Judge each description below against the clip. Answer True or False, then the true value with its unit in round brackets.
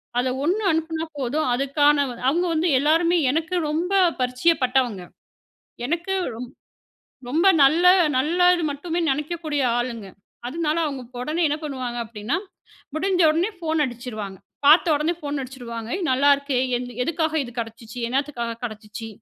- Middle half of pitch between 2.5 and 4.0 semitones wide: False (4.6 semitones)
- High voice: True (285 Hz)